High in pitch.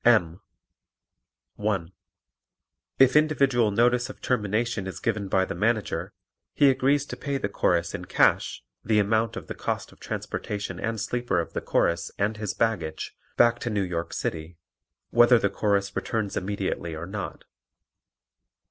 No: low, 105 Hz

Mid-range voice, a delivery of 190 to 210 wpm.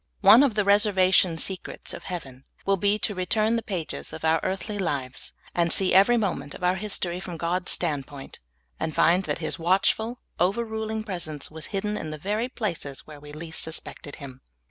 Yes: medium, 180 Hz; average, 195 wpm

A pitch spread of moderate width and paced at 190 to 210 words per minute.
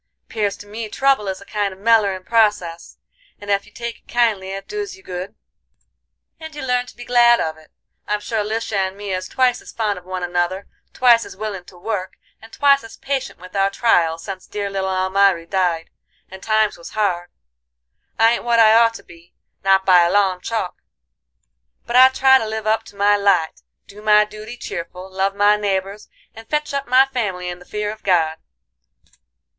Yes: average, 3.4 semitones; average, 200 wpm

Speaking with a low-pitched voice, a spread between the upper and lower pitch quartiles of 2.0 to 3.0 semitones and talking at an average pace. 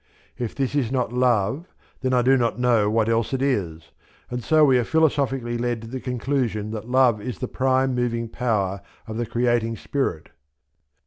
Yes: low, 120 Hz; narrow, 2.5 semitones; average, 185 wpm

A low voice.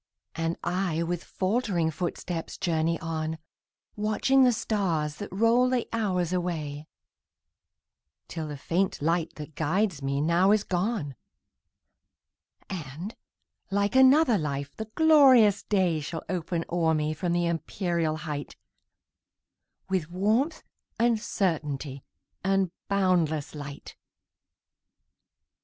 No: medium, 175 Hz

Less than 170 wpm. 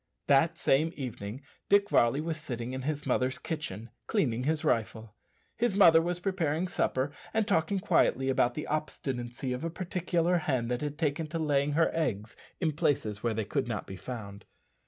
No: average, 175 wpm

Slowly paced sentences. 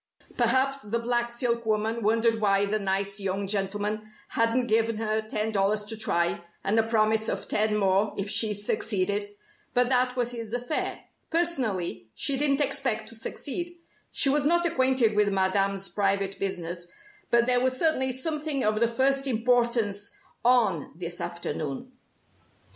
No: average, 155 wpm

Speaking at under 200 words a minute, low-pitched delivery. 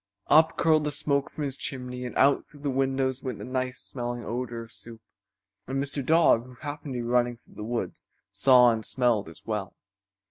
No: fast, 205 wpm; low, 125 Hz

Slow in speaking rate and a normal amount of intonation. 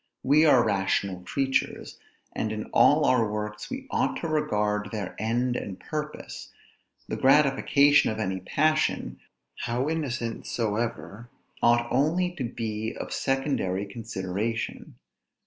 Yes: slow, 125 wpm; average, 4.9 semitones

